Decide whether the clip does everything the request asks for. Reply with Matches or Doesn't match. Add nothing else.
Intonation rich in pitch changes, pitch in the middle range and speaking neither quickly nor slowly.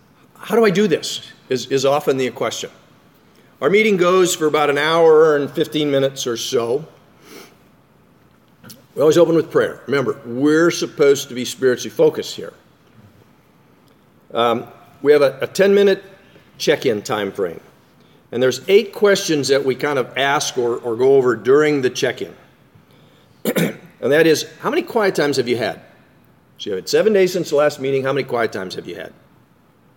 Matches